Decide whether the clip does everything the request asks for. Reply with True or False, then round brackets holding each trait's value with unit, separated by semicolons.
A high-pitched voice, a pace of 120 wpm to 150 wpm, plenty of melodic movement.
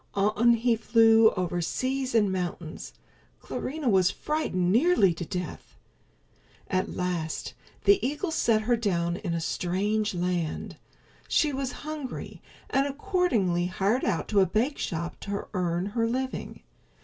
True (210 Hz; 135 wpm; 6.1 semitones)